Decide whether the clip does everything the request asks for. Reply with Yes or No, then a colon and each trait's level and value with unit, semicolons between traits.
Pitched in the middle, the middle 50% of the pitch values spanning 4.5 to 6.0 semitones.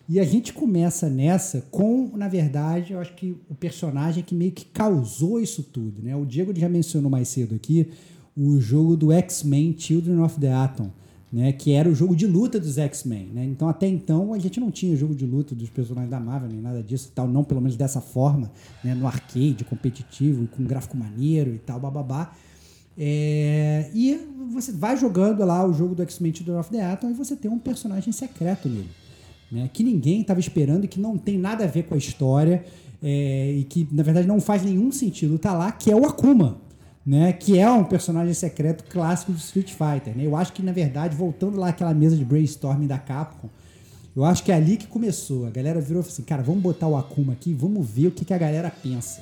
Yes: medium, 160 Hz; average, 5.2 semitones